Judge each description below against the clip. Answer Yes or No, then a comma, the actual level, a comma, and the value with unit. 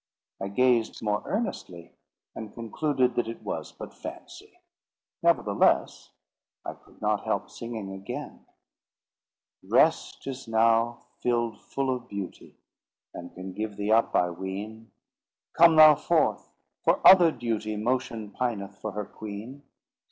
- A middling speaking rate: No, slow, 130 wpm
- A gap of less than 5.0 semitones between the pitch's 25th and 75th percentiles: Yes, average, 3.7 semitones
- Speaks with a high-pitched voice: No, low, 115 Hz